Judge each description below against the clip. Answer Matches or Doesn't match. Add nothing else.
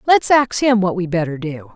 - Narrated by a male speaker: Doesn't match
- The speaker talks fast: Matches